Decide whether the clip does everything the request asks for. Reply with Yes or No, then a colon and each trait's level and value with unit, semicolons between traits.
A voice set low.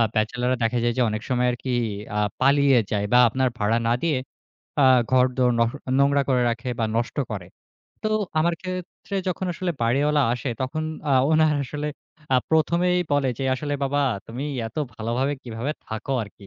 Yes: low, 130 Hz